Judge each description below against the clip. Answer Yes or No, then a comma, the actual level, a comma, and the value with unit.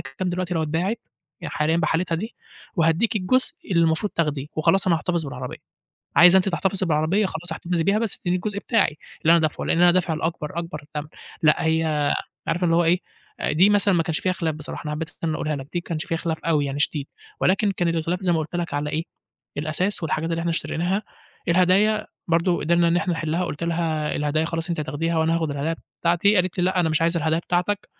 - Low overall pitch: No, medium, 165 Hz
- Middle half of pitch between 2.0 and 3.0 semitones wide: Yes, narrow, 2.4 semitones